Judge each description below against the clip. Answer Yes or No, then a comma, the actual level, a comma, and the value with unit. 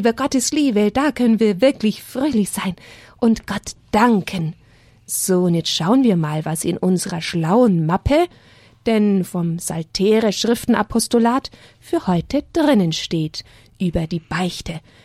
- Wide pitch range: Yes, wide, 6.1 semitones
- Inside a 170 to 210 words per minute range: No, average, 130 wpm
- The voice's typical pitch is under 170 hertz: No, high, 190 Hz